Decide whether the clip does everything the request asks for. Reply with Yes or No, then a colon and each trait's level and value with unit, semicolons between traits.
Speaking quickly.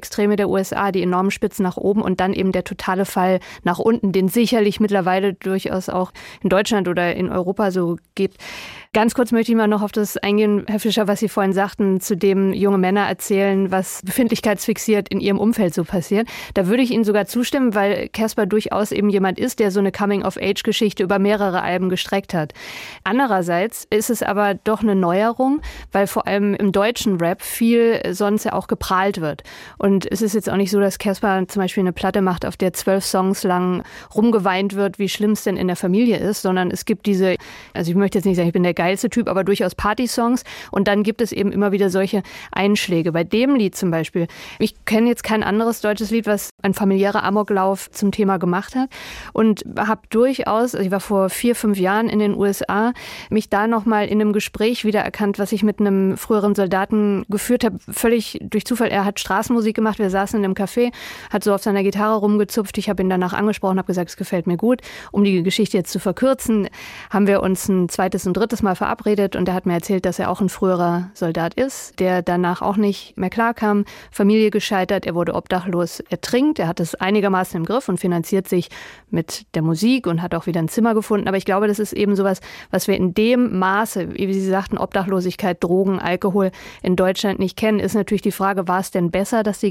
Yes: fast, 215 wpm